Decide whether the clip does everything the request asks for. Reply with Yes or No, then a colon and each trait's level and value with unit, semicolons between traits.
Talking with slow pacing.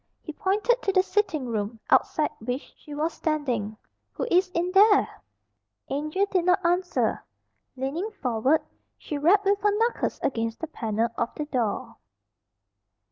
No: average, 145 wpm